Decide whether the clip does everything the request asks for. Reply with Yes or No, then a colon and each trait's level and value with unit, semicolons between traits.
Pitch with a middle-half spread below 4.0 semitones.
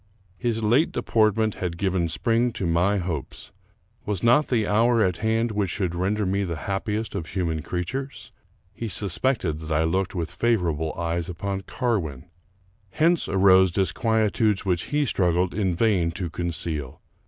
No: average, 4.5 semitones